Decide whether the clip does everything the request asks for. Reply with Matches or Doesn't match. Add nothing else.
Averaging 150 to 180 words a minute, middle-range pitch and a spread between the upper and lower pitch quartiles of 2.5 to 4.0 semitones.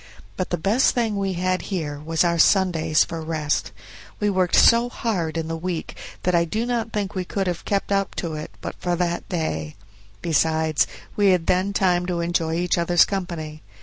Doesn't match